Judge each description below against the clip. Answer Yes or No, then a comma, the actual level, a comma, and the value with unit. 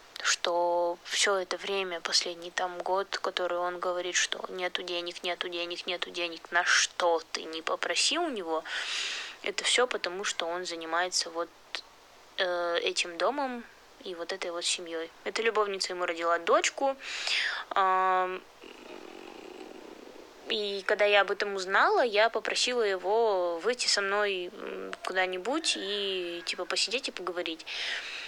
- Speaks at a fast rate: No, average, 135 wpm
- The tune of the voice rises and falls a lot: No, average, 3.6 semitones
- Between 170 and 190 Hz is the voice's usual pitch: Yes, medium, 185 Hz